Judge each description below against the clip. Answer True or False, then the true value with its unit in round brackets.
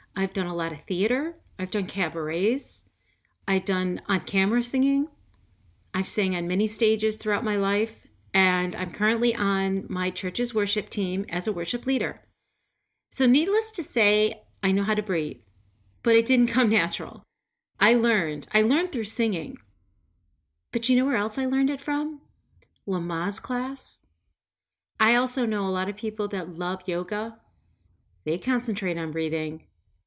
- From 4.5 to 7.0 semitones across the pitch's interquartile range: True (5.6 semitones)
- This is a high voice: True (195 Hz)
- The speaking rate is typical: True (160 wpm)